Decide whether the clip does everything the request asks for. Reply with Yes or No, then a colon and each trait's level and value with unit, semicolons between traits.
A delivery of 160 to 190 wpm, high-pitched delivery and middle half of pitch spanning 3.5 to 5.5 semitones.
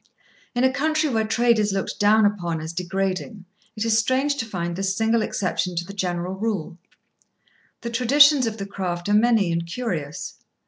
Yes: average, 180 wpm; high, 205 Hz; average, 4.4 semitones